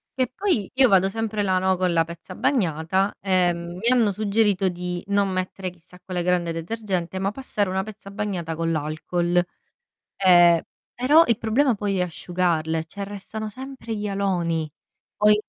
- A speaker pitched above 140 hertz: Yes, high, 190 Hz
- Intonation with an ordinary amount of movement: Yes, average, 3.2 semitones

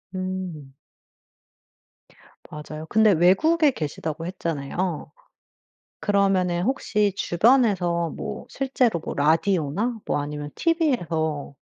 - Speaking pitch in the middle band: Yes, medium, 180 Hz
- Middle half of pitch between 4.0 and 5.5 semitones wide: Yes, average, 5.2 semitones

